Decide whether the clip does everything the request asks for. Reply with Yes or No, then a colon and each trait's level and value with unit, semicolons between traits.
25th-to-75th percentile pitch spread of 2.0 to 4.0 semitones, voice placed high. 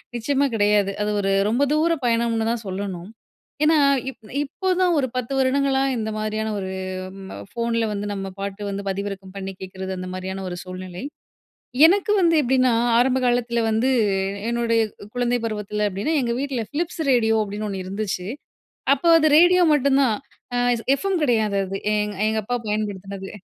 No: average, 4.6 semitones; high, 220 Hz